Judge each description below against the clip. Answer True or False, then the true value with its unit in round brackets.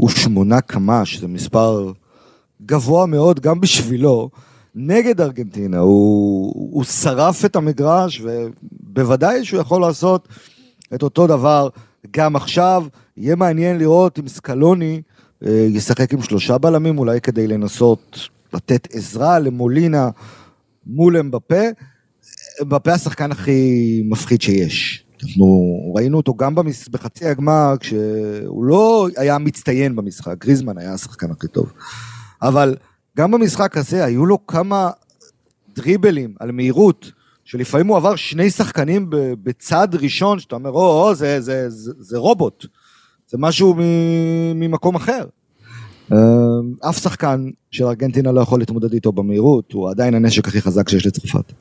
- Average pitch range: False (6.3 semitones)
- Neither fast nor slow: True (130 wpm)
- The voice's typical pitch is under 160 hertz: True (135 Hz)